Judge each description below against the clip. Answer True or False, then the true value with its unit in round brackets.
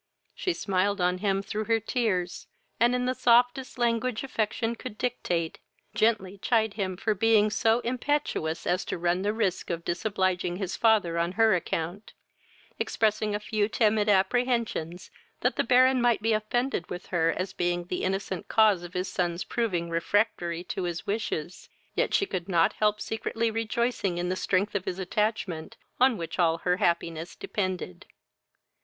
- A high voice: True (205 Hz)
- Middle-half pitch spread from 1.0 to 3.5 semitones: False (4.1 semitones)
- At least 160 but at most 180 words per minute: True (165 wpm)